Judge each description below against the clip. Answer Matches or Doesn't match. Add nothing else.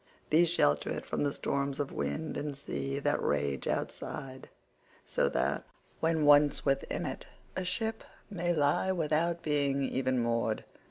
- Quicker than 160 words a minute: Doesn't match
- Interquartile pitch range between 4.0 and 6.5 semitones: Doesn't match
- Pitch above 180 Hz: Doesn't match